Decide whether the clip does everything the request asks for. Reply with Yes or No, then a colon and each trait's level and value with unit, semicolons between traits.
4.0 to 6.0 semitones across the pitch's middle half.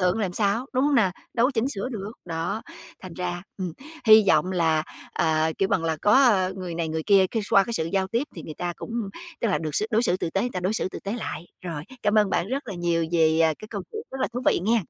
Yes: average, 4.6 semitones